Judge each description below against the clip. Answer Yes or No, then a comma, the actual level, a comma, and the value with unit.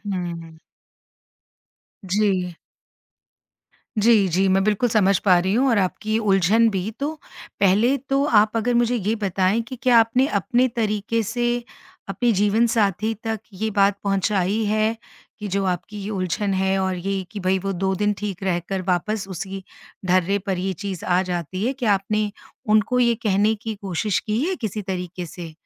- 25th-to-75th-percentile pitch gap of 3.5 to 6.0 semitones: No, average, 2.9 semitones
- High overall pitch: Yes, high, 200 Hz